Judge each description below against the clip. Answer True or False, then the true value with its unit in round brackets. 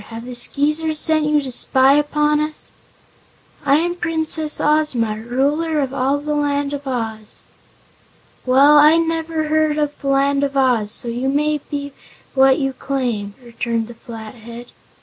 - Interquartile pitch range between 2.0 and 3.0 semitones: False (3.7 semitones)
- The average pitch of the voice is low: False (280 Hz)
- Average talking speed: True (155 wpm)